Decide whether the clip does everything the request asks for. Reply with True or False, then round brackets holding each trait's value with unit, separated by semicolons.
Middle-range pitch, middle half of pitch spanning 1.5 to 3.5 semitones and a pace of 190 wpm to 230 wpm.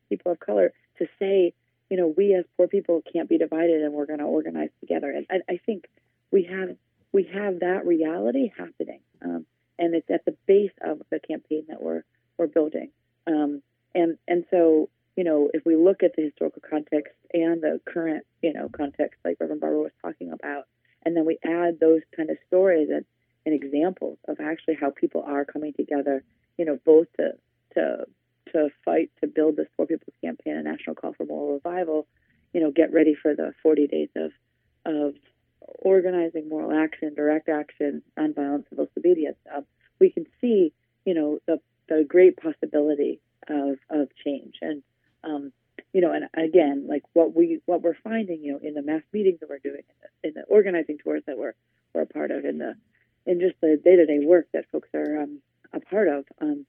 True (155 Hz; 3.2 semitones; 195 wpm)